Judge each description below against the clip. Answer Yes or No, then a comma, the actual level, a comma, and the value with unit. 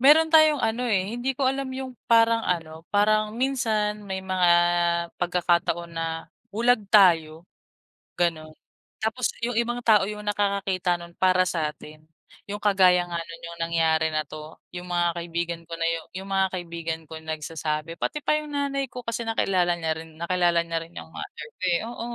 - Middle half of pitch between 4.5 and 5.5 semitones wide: Yes, average, 4.9 semitones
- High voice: No, medium, 180 Hz